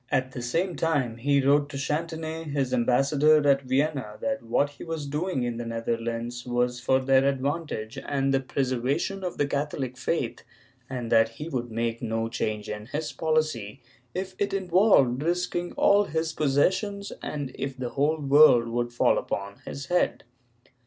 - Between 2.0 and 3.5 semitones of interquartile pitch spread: No, average, 4.3 semitones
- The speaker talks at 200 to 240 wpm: No, average, 165 wpm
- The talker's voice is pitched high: No, low, 135 Hz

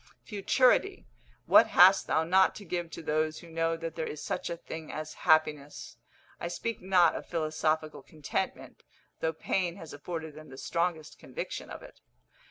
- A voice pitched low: No, medium, 165 Hz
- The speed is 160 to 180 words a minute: Yes, average, 170 wpm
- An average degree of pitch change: No, narrow, 2.3 semitones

